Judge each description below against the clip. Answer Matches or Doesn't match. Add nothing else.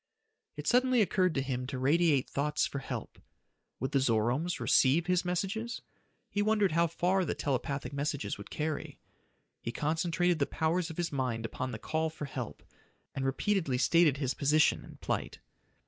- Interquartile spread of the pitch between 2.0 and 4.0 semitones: Doesn't match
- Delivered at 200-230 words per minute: Doesn't match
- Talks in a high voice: Doesn't match